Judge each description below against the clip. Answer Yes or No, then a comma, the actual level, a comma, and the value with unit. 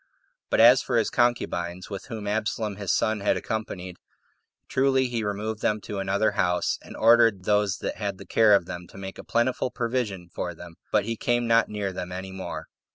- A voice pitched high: No, low, 105 Hz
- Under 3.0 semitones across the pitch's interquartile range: No, average, 3.3 semitones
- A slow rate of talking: No, average, 200 wpm